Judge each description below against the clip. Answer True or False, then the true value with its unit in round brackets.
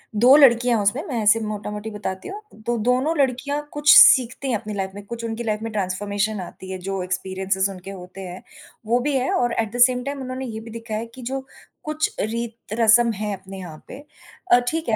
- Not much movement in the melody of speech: False (3.9 semitones)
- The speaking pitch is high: True (225 Hz)